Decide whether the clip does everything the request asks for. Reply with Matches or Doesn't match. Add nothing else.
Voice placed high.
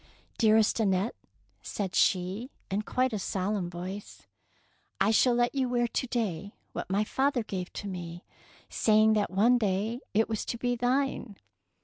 Matches